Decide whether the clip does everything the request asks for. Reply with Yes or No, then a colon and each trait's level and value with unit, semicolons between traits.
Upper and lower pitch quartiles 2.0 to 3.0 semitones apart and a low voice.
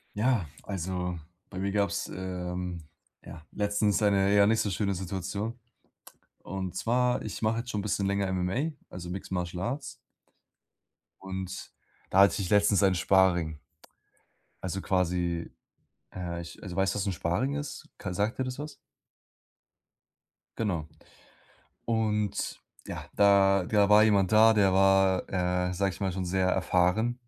Yes: narrow, 2.4 semitones; very low, 95 Hz